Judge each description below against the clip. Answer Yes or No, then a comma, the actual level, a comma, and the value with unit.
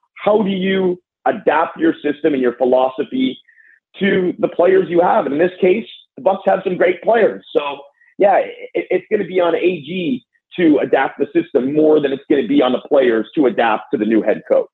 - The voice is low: No, high, 190 Hz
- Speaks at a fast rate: Yes, fast, 210 wpm